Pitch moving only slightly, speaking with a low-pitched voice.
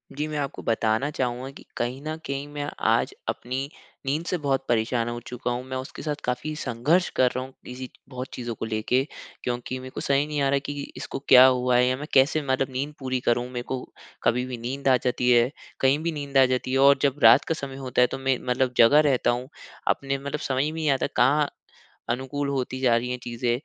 Yes: narrow, 2.1 semitones; low, 130 Hz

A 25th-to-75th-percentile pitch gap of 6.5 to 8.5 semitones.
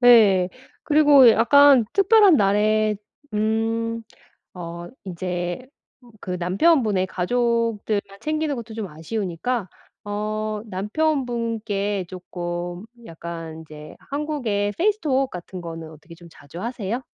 No: average, 5.3 semitones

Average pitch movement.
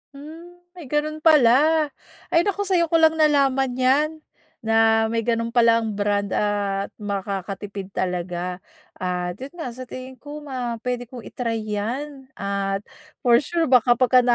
No: wide, 6.2 semitones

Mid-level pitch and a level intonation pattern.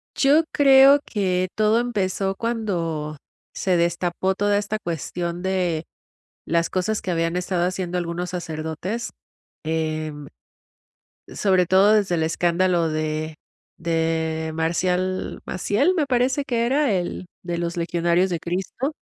No: medium, 180 Hz; average, 3.6 semitones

